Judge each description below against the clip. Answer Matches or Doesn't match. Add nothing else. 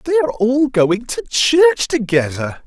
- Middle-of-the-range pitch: Matches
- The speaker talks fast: Doesn't match